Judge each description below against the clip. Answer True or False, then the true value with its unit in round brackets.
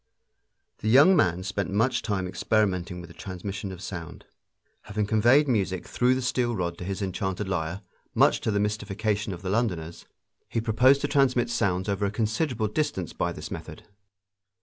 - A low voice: True (105 Hz)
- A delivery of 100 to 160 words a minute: False (170 wpm)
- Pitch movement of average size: True (4.0 semitones)